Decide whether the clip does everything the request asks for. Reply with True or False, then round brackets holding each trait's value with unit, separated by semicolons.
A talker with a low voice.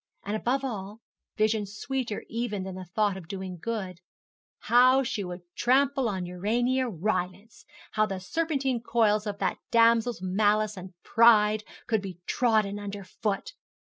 False (215 Hz)